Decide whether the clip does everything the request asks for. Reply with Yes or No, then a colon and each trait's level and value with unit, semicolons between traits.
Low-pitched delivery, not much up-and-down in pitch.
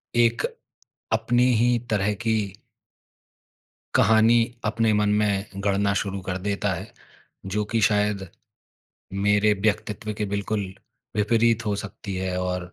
Yes: low, 105 Hz; narrow, 1.9 semitones